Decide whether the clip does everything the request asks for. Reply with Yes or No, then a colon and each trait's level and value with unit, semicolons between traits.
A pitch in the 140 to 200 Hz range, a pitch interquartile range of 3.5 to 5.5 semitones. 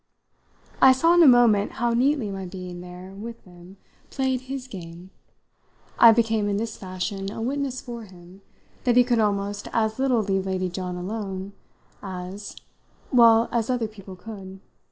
No: high, 210 Hz; average, 4.1 semitones